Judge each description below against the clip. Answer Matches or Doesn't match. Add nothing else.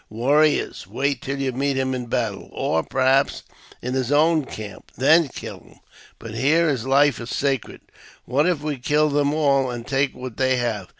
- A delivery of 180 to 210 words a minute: Matches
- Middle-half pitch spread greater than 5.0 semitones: Doesn't match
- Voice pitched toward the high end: Doesn't match